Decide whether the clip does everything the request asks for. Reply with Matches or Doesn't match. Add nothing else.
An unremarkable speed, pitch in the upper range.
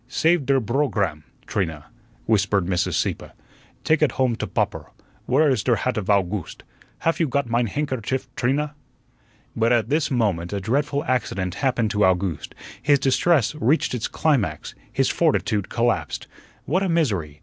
Doesn't match